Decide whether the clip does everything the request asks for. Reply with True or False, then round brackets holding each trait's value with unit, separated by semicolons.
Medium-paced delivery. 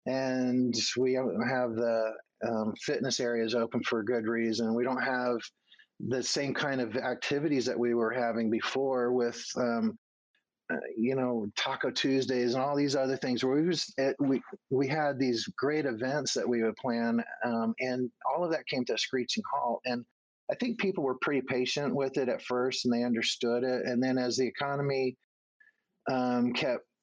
True (185 wpm)